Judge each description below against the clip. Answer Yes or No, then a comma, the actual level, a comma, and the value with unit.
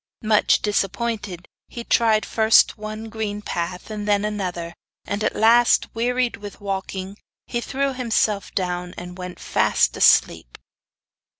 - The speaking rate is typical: No, slow, 130 wpm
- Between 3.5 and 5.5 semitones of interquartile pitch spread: No, average, 3.1 semitones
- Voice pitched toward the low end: No, high, 210 Hz